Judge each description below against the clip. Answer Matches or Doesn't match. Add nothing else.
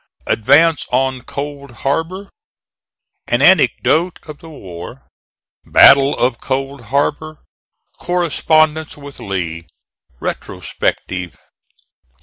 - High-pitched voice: Doesn't match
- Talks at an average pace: Doesn't match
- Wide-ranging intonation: Doesn't match